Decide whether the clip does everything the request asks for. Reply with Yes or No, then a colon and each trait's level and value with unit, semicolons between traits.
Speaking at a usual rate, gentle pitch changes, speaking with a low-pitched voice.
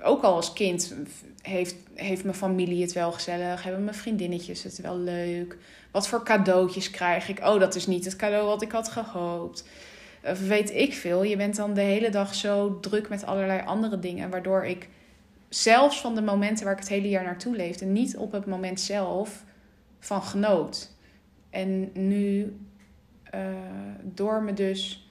No: average, 175 wpm; narrow, 2.3 semitones; high, 195 Hz